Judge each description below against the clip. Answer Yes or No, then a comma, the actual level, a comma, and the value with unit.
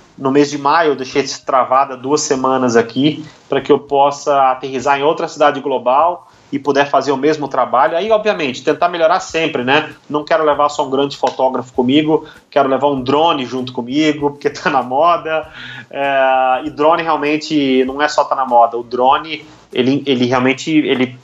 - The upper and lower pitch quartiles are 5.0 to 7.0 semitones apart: No, narrow, 2.6 semitones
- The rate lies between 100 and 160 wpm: No, fast, 185 wpm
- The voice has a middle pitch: Yes, medium, 145 Hz